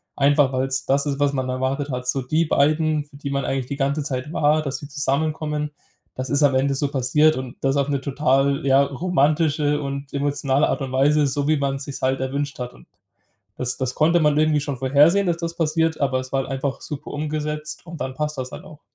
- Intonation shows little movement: Yes, narrow, 2.1 semitones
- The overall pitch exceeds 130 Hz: Yes, medium, 140 Hz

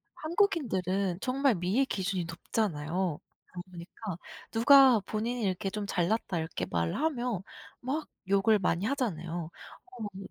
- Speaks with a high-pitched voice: Yes, high, 200 Hz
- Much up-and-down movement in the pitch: Yes, wide, 5.7 semitones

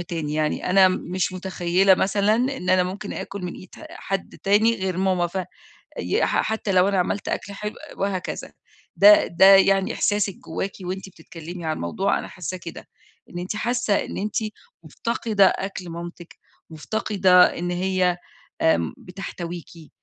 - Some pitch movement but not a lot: No, narrow, 2.1 semitones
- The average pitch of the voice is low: No, medium, 185 Hz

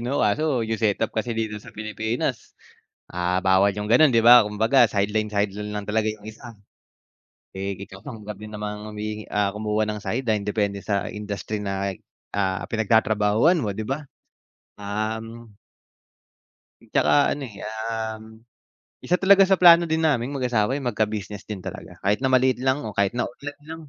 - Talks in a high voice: No, low, 110 Hz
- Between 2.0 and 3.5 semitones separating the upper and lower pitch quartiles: Yes, average, 2.7 semitones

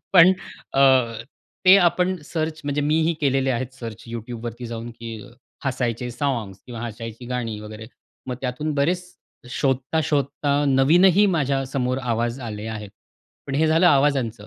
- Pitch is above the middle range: No, low, 130 Hz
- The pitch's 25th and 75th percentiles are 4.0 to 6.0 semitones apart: Yes, average, 4.7 semitones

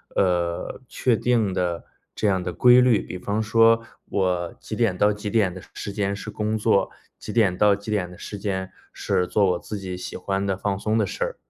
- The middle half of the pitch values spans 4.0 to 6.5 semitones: No, average, 2.8 semitones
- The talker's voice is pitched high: No, low, 100 Hz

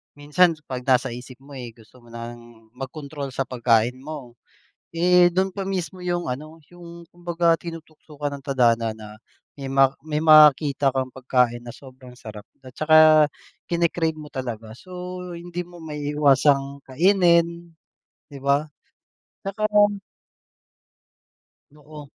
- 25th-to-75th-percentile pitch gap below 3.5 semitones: No, average, 4.8 semitones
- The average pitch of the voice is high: No, medium, 145 Hz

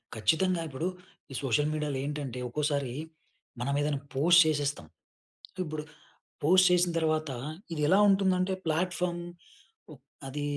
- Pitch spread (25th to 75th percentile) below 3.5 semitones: No, average, 3.8 semitones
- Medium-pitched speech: Yes, medium, 155 Hz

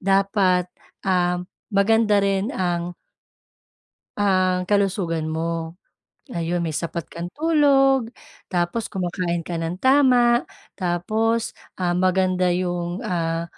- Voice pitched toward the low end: No, medium, 185 Hz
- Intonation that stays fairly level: No, average, 3.0 semitones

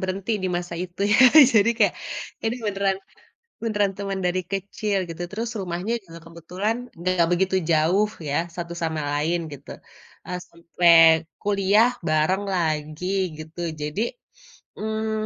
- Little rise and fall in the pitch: No, average, 3.2 semitones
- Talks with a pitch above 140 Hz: Yes, medium, 185 Hz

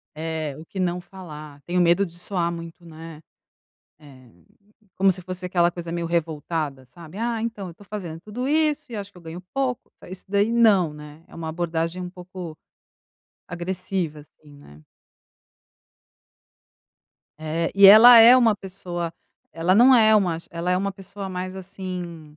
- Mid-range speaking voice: Yes, medium, 180 Hz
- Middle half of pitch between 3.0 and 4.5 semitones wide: Yes, average, 3.3 semitones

